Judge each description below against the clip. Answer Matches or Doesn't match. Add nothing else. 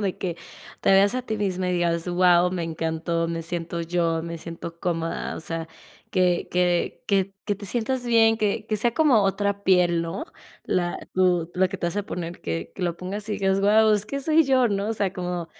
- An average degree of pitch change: Matches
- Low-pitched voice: Doesn't match